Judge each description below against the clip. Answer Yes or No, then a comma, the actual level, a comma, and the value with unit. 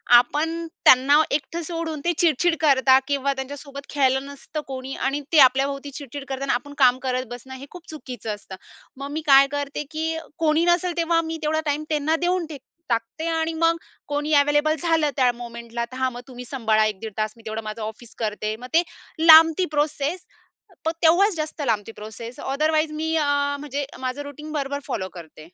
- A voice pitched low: No, very high, 285 Hz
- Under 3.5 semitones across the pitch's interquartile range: No, average, 3.9 semitones